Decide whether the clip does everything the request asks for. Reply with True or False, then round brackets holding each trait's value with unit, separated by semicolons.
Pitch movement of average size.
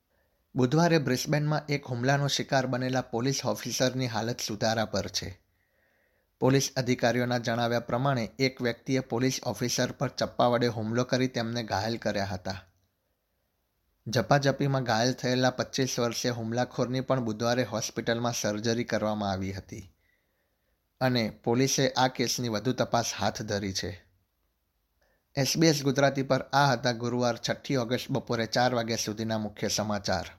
True (3.3 semitones)